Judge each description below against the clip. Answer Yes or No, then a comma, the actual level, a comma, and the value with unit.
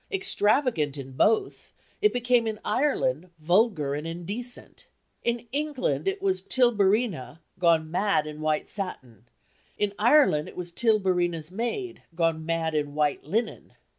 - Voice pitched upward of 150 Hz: Yes, high, 190 Hz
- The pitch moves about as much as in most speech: No, wide, 7.4 semitones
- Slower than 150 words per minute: Yes, slow, 135 wpm